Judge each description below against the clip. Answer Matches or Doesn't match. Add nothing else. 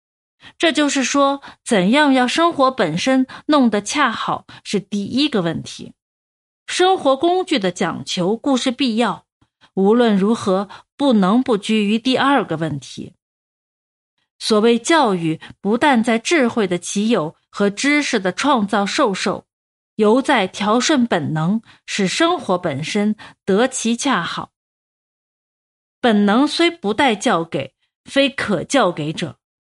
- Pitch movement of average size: Doesn't match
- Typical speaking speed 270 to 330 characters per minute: Doesn't match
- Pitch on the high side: Matches